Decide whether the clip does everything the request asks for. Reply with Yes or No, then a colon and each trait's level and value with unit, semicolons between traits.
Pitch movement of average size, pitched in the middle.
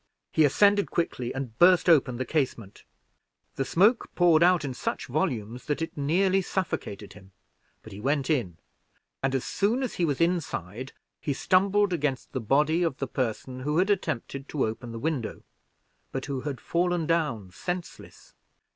No: wide, 5.7 semitones; medium, 145 Hz